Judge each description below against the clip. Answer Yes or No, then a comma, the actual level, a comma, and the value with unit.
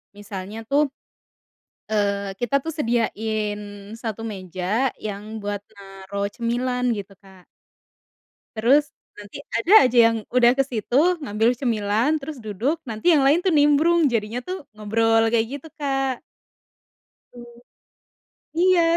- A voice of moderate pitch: No, high, 230 Hz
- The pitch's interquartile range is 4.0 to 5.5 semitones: Yes, average, 4.7 semitones